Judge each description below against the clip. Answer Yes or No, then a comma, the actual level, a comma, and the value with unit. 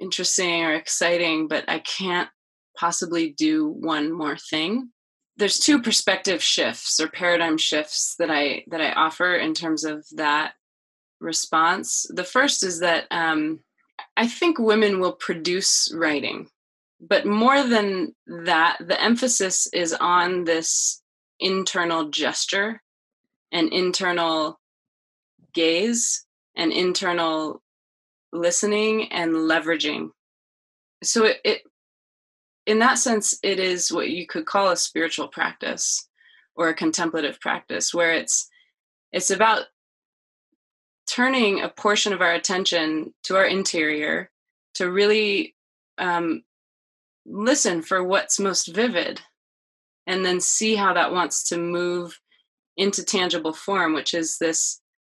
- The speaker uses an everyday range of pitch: Yes, average, 4.5 semitones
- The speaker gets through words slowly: Yes, slow, 120 wpm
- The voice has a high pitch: No, medium, 180 Hz